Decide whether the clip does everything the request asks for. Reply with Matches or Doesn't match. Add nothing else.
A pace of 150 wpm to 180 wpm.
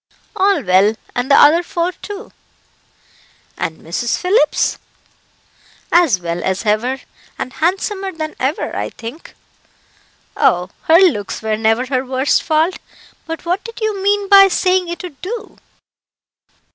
Doesn't match